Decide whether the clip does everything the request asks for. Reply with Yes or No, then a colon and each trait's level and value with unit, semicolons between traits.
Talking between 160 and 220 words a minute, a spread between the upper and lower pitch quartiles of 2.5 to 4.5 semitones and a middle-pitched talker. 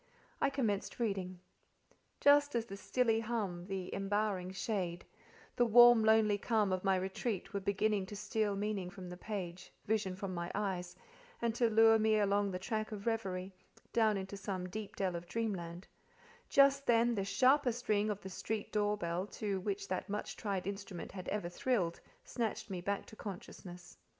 No: average, 170 wpm; average, 2.9 semitones; high, 205 Hz